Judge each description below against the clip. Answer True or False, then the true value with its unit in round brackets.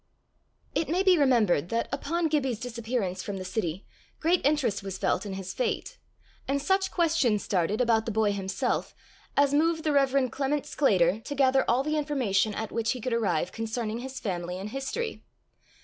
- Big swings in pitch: True (5.9 semitones)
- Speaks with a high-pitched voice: True (240 Hz)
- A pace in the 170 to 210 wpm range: True (180 wpm)